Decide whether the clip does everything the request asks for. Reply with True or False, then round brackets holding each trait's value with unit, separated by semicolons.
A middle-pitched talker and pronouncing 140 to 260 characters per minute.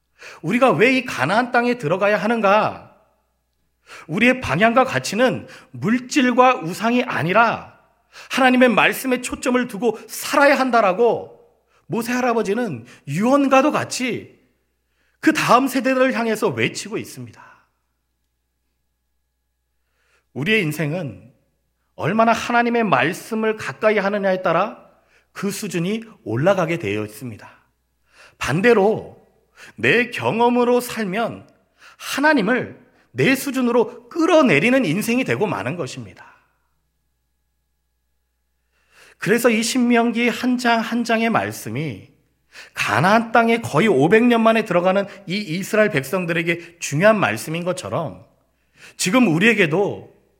False (215 Hz; 255 characters per minute)